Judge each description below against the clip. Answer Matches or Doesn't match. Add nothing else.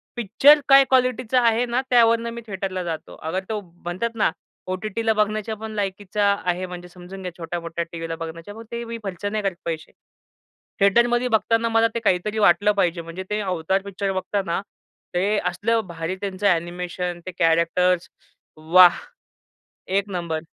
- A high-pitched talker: Matches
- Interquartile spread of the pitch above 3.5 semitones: Matches